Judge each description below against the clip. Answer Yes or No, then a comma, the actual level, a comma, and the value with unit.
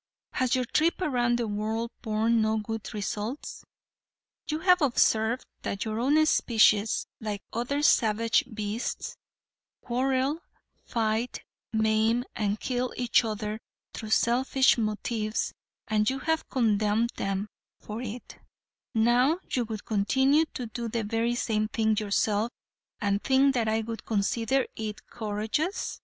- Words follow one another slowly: Yes, slow, 130 wpm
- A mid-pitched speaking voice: No, high, 225 Hz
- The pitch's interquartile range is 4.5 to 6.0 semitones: No, narrow, 2.6 semitones